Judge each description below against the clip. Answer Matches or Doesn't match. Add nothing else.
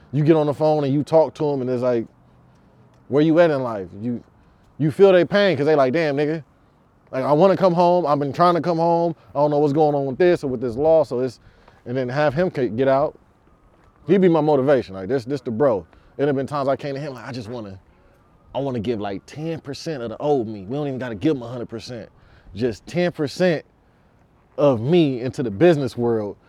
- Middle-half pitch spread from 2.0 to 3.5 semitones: Doesn't match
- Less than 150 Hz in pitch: Matches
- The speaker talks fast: Matches